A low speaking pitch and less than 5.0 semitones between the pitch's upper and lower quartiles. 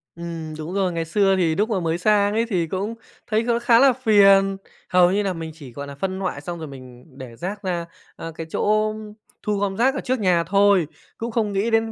No: high, 195 Hz; average, 4.4 semitones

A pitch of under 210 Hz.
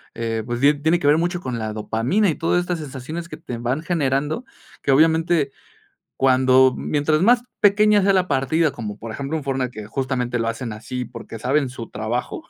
Yes: low, 135 Hz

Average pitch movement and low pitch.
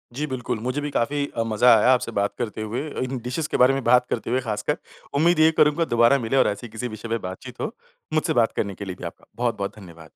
Yes: average, 4.0 semitones; low, 120 Hz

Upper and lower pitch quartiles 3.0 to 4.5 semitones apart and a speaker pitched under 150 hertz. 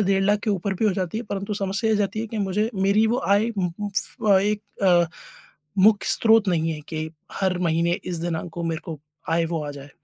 No: average, 3.5 semitones; high, 195 Hz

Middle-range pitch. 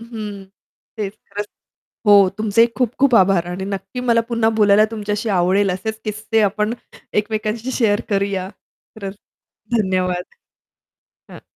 No: high, 210 Hz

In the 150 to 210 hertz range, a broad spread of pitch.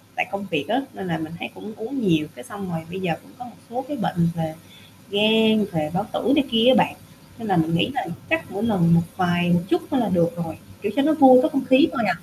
Yes: high, 205 Hz; wide, 7.0 semitones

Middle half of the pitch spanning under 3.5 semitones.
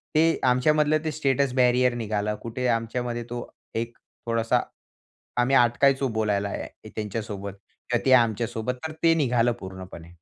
Yes: average, 2.8 semitones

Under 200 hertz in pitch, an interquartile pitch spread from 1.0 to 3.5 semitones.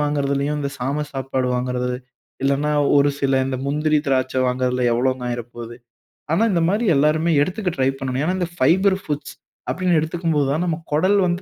No: medium, 140 Hz; average, 4.0 semitones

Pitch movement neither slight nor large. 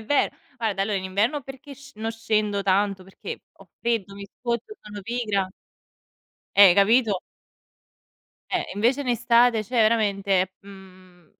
Yes: average, 3.3 semitones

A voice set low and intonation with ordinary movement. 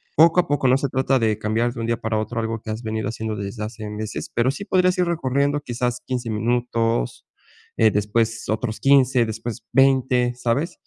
Yes: low, 120 Hz; average, 3.2 semitones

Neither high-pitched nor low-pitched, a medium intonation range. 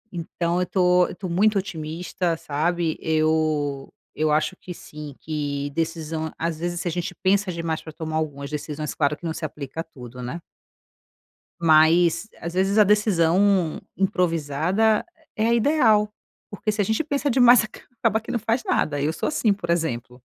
Yes: medium, 170 Hz; average, 4.2 semitones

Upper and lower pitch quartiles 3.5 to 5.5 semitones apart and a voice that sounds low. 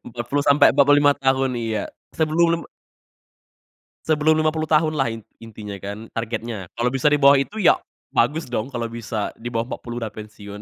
Yes: average, 4.7 semitones; low, 125 Hz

